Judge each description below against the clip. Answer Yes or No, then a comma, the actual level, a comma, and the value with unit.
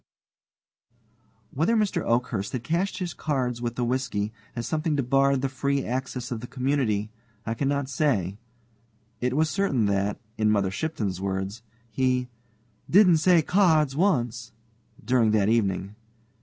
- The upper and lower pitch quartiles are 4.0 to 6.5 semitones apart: Yes, average, 5.2 semitones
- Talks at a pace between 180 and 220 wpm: No, average, 140 wpm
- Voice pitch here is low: Yes, low, 125 Hz